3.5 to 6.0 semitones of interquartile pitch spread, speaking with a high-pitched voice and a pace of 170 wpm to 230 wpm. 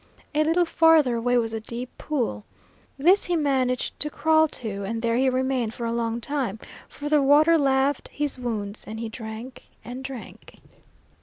Yes: average, 4.2 semitones; very high, 255 Hz; average, 175 wpm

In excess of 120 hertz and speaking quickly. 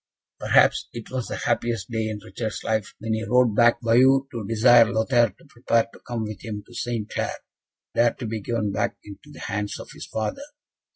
No: low, 115 Hz; fast, 210 wpm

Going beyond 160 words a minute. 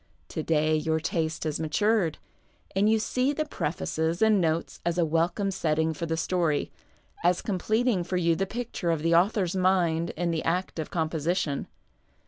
Yes: average, 175 wpm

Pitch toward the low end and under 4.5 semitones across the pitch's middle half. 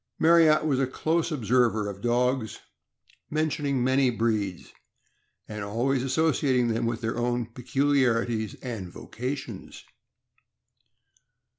Yes: low, 125 Hz; average, 3.4 semitones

